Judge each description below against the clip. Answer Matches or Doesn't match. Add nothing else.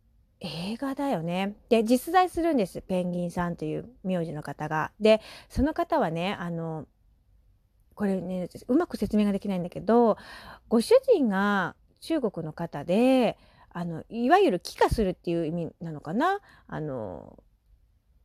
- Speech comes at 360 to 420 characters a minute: Doesn't match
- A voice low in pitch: Doesn't match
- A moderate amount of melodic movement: Doesn't match